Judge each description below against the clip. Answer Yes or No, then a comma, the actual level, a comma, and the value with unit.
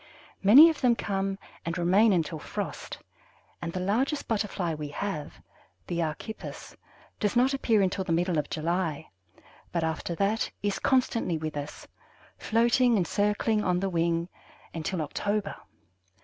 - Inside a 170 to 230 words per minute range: No, average, 145 wpm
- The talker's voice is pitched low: No, high, 190 Hz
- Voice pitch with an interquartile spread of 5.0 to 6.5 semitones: No, average, 4.6 semitones